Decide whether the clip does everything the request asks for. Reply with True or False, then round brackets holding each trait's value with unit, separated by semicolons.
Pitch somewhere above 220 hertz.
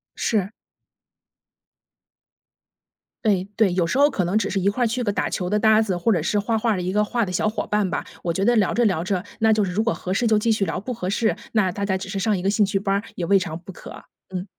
False (200 Hz)